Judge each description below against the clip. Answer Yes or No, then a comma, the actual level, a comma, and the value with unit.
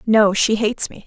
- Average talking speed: No, fast, 225 wpm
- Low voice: No, high, 215 Hz